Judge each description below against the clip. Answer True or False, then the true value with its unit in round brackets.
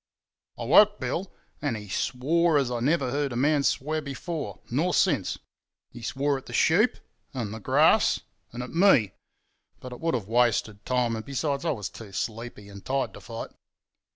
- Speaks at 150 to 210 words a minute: True (180 wpm)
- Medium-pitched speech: False (130 Hz)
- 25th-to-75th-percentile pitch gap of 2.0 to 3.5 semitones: False (4.7 semitones)